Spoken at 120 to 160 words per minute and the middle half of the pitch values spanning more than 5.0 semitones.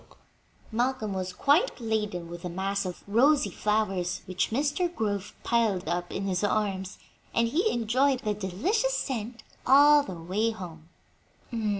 Yes: average, 140 wpm; wide, 5.5 semitones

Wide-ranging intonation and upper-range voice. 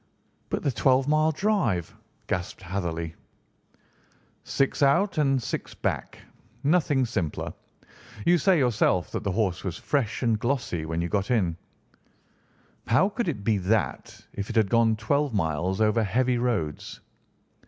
No: wide, 6.9 semitones; low, 110 Hz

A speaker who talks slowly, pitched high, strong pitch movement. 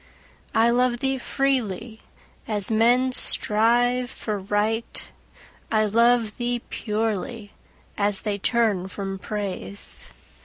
No: slow, 105 wpm; high, 225 Hz; average, 2.7 semitones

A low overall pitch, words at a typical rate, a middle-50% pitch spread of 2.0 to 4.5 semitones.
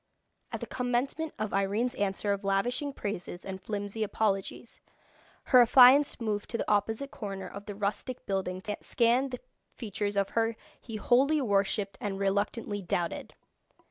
No: high, 210 Hz; average, 150 wpm; average, 3.6 semitones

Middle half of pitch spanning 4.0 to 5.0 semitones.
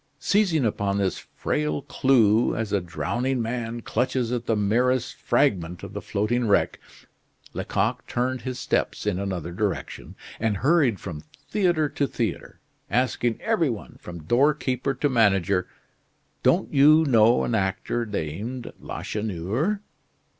Yes: average, 4.6 semitones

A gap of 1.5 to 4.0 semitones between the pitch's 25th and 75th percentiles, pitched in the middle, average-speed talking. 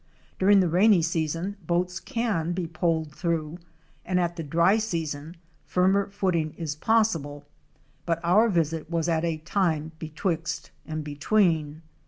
Yes: average, 2.9 semitones; medium, 170 Hz; average, 145 wpm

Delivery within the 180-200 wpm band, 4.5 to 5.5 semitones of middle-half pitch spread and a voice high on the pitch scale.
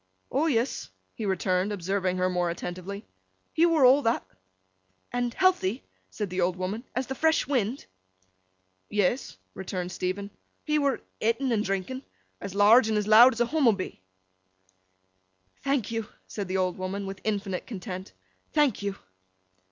No: average, 145 wpm; average, 5.1 semitones; high, 210 Hz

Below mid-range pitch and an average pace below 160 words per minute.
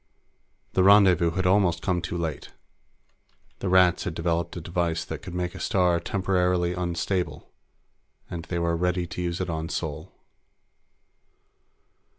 Yes: very low, 90 Hz; average, 145 wpm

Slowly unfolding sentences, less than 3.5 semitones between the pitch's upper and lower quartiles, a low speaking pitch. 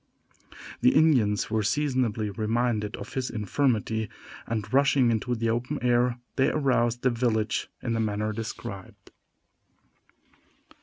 Yes: slow, 120 wpm; average, 2.9 semitones; low, 115 Hz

